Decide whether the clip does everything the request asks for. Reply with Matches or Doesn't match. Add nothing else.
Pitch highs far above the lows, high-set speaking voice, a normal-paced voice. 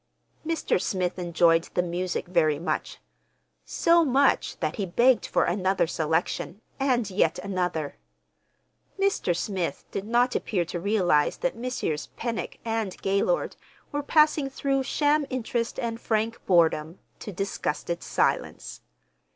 Doesn't match